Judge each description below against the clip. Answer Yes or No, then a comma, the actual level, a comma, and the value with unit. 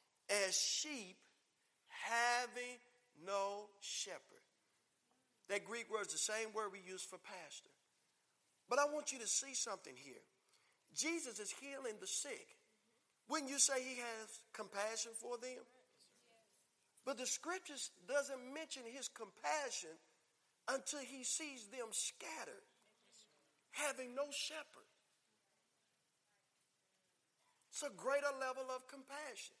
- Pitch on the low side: No, very high, 255 Hz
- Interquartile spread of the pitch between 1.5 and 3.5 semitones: No, average, 4.8 semitones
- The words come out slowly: Yes, slow, 120 wpm